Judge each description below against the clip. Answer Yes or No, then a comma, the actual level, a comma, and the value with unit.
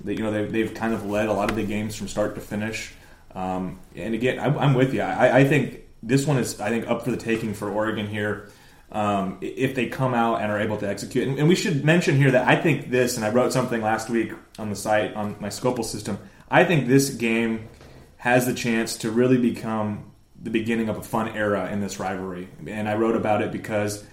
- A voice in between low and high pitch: No, low, 110 Hz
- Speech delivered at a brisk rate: Yes, fast, 240 wpm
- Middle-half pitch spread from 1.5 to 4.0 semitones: Yes, average, 2.9 semitones